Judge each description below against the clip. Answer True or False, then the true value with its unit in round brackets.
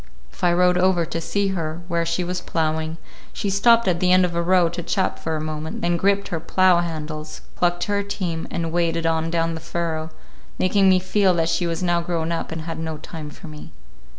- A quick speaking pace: True (230 wpm)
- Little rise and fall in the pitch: True (2.1 semitones)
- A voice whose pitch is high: False (170 Hz)